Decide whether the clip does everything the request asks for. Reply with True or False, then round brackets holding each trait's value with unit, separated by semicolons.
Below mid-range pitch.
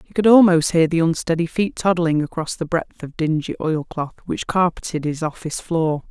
False (165 Hz)